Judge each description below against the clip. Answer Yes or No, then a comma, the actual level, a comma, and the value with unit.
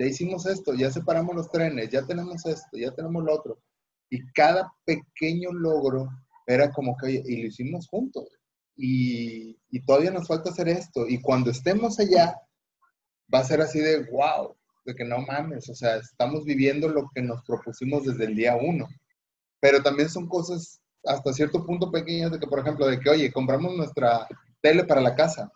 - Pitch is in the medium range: Yes, medium, 150 Hz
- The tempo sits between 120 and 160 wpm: No, average, 185 wpm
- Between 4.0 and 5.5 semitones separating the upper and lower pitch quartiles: Yes, average, 4.6 semitones